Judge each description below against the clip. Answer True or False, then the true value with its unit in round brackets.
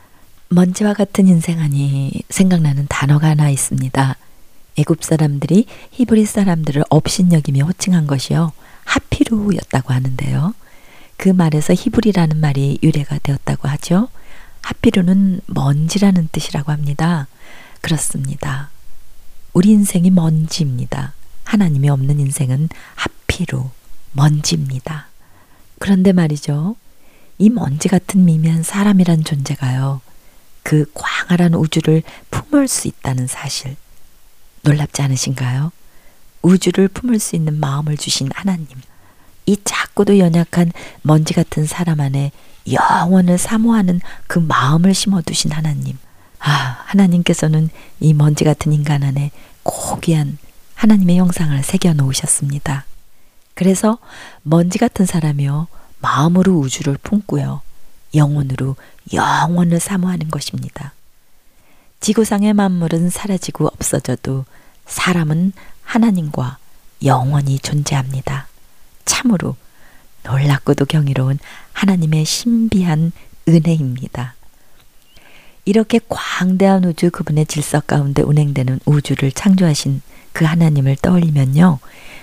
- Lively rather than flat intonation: False (4.6 semitones)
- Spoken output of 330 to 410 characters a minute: False (275 characters per minute)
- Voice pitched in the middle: True (155 Hz)